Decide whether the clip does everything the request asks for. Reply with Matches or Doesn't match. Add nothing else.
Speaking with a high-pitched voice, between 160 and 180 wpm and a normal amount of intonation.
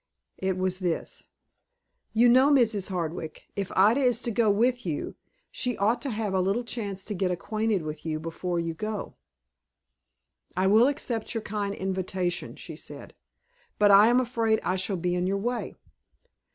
Matches